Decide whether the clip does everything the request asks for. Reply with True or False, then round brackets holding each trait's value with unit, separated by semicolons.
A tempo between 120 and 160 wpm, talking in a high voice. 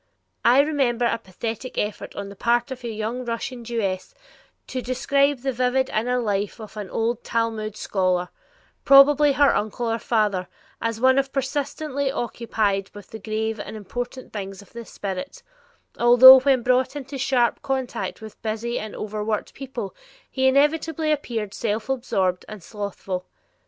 True (155 wpm; 235 Hz)